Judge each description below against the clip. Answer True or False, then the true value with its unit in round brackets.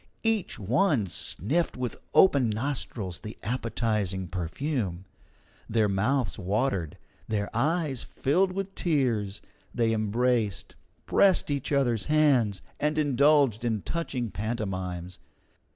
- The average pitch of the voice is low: True (115 Hz)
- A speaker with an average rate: False (105 wpm)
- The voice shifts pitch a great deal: True (5.9 semitones)